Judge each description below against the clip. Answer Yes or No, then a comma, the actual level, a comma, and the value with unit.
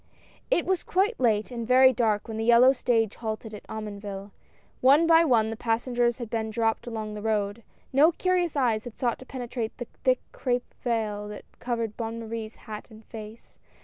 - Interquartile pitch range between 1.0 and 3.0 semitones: Yes, narrow, 2.6 semitones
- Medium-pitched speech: No, high, 230 Hz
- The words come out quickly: No, average, 195 wpm